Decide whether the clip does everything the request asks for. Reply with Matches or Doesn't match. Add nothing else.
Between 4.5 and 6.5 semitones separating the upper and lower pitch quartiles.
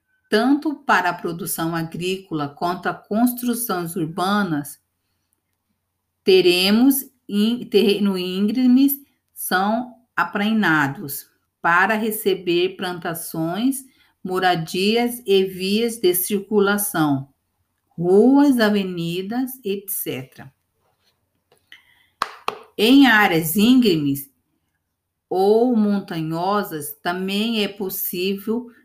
Matches